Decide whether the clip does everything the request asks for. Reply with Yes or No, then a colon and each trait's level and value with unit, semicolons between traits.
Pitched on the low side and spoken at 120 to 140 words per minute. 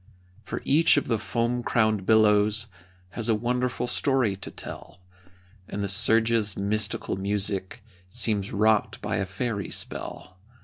Yes: low, 110 Hz; slow, 135 wpm